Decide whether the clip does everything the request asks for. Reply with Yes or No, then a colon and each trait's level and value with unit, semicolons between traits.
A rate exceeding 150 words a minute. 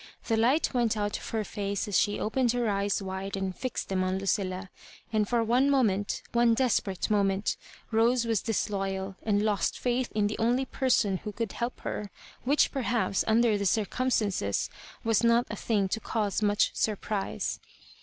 Yes: average, 175 wpm